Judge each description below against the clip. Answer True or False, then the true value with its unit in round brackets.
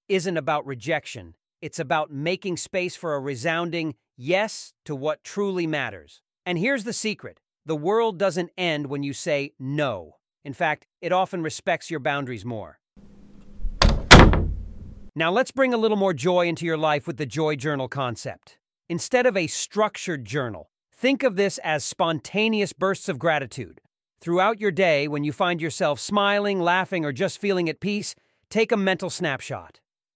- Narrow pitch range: False (5.0 semitones)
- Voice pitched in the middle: True (165 Hz)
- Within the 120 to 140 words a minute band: False (160 wpm)